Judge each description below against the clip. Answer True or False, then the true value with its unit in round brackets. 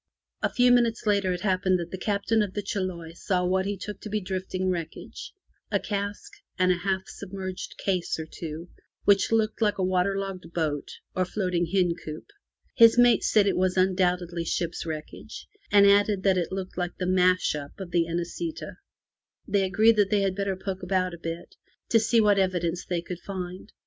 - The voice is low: False (185 Hz)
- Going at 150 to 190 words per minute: False (200 wpm)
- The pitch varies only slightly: True (2.2 semitones)